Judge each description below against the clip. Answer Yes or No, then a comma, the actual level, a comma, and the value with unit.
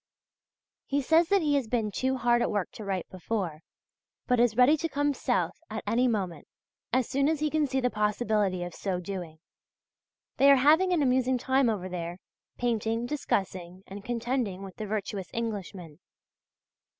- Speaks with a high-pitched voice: Yes, high, 230 Hz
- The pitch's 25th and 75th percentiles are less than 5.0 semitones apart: No, wide, 5.4 semitones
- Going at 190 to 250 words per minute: No, average, 175 wpm